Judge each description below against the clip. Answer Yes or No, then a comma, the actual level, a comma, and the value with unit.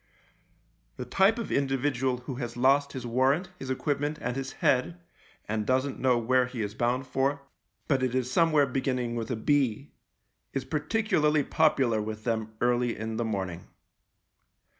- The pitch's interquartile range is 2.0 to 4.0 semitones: Yes, average, 3.0 semitones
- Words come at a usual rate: Yes, average, 160 wpm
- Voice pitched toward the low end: Yes, low, 130 Hz